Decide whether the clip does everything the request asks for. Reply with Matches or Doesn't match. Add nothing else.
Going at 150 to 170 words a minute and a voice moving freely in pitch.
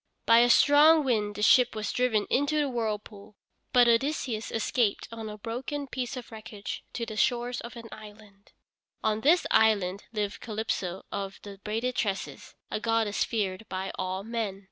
Doesn't match